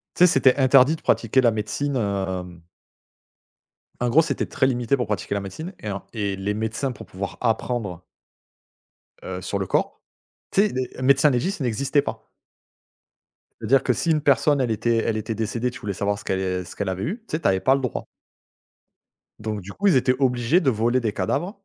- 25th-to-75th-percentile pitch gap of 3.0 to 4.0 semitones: No, average, 5.1 semitones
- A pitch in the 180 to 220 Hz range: No, low, 120 Hz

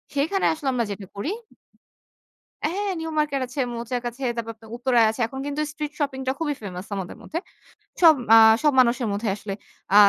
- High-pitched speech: Yes, very high, 260 Hz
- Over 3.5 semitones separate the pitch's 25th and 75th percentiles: Yes, average, 4.7 semitones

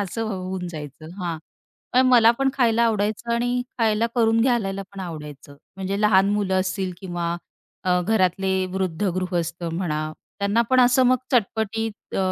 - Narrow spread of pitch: No, average, 4.0 semitones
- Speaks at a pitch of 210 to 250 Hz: No, high, 195 Hz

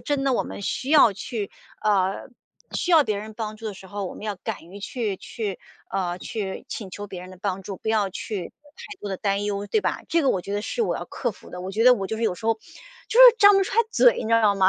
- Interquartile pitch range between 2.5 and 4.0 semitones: Yes, average, 3.4 semitones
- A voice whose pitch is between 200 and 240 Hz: Yes, high, 210 Hz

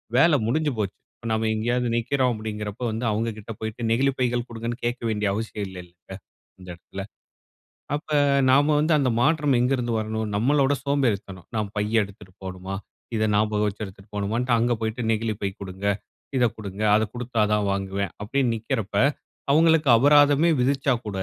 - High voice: No, low, 115 Hz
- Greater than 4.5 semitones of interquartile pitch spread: No, average, 3.8 semitones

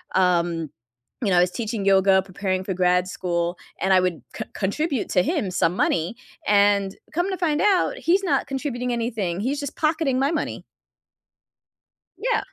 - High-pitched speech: Yes, high, 200 Hz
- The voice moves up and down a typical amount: No, wide, 7.7 semitones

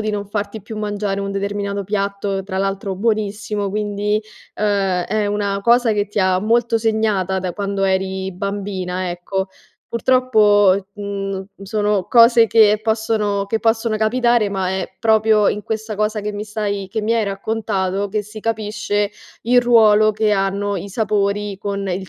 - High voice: Yes, high, 205 Hz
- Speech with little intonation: Yes, narrow, 1.6 semitones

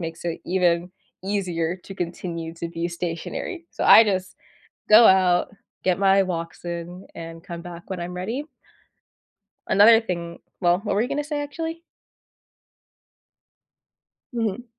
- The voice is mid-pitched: Yes, medium, 180 Hz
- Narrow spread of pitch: No, average, 3.3 semitones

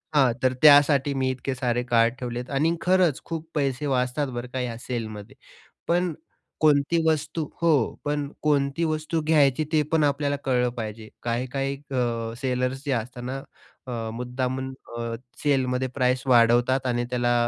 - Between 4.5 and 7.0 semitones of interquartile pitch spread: No, average, 2.9 semitones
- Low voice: Yes, low, 130 Hz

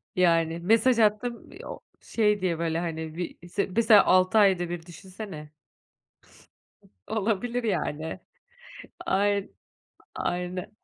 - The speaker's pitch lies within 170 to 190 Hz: Yes, medium, 185 Hz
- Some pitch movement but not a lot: Yes, average, 3.9 semitones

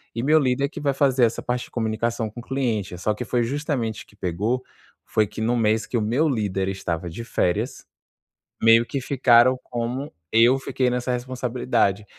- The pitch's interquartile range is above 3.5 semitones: No, average, 2.9 semitones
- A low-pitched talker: Yes, low, 120 Hz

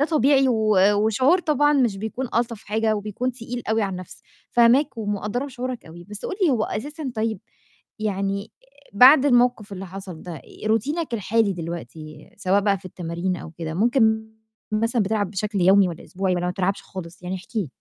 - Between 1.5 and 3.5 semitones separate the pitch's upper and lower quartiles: No, average, 4.3 semitones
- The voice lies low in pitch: No, high, 215 Hz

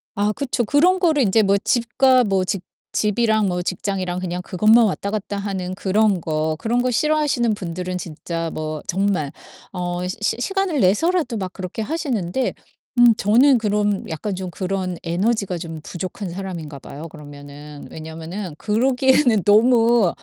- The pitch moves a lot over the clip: No, average, 4.9 semitones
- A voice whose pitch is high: Yes, high, 200 Hz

